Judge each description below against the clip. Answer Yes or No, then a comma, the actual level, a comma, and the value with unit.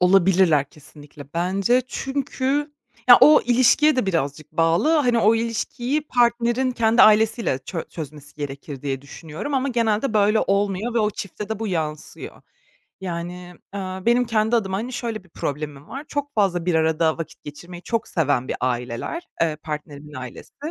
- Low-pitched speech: No, high, 195 Hz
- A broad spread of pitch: Yes, wide, 7.3 semitones